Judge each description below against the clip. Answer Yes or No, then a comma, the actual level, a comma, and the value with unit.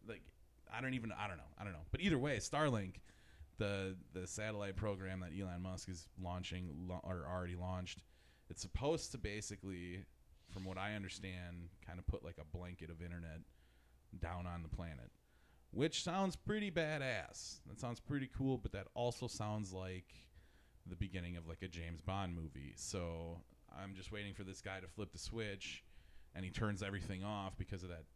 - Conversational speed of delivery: Yes, average, 190 wpm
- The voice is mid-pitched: No, very low, 95 Hz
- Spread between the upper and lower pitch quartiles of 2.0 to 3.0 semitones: No, average, 3.5 semitones